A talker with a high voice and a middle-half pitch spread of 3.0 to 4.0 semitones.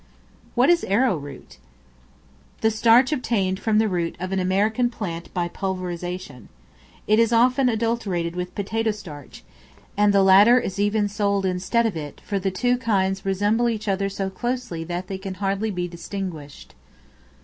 Yes: high, 195 Hz; average, 3.5 semitones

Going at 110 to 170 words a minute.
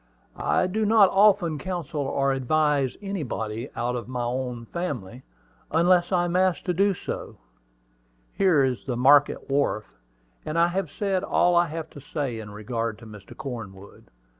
Yes: average, 165 wpm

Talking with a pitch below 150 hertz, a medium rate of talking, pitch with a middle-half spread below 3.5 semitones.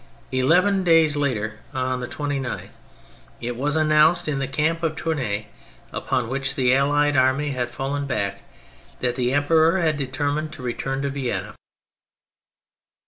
Yes: medium, 140 Hz; average, 145 wpm; average, 3.1 semitones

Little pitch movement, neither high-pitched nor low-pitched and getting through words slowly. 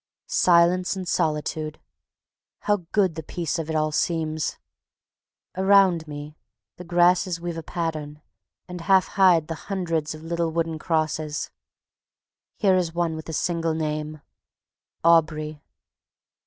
Yes: narrow, 2.2 semitones; medium, 165 Hz; slow, 130 wpm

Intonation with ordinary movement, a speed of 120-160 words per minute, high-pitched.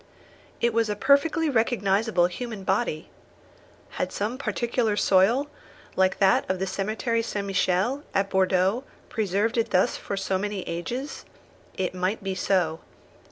Yes: average, 3.6 semitones; average, 140 wpm; high, 200 Hz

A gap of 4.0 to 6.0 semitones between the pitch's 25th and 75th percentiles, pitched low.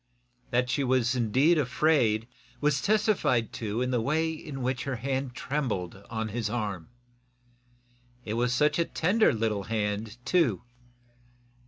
Yes: average, 4.7 semitones; low, 125 Hz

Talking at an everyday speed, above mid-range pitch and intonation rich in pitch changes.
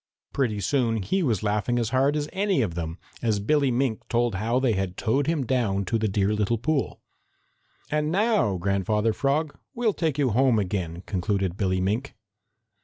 No: average, 180 wpm; low, 115 Hz; wide, 5.8 semitones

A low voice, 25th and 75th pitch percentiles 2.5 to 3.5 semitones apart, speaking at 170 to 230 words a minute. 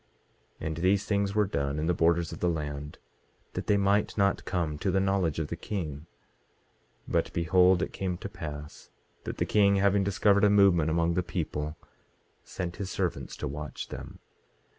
No: very low, 90 Hz; average, 4.1 semitones; average, 185 wpm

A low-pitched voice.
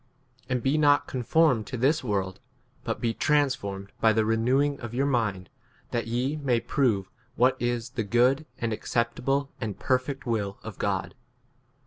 Yes: low, 120 Hz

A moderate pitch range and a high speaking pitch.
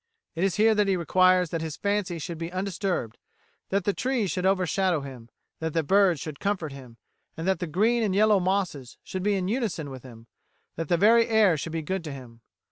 No: average, 4.1 semitones; medium, 180 Hz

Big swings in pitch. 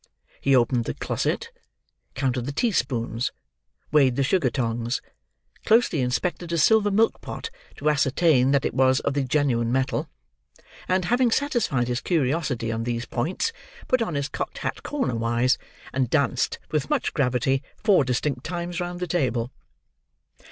Yes: wide, 5.9 semitones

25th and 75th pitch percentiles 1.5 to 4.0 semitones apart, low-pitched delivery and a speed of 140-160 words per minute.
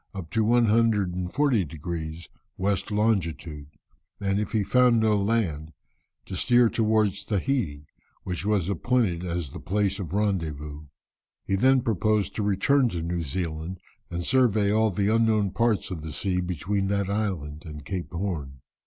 No: average, 4.4 semitones; low, 100 Hz; average, 150 wpm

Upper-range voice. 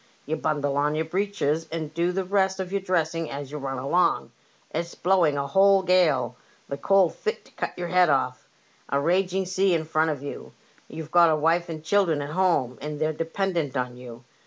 No: medium, 160 Hz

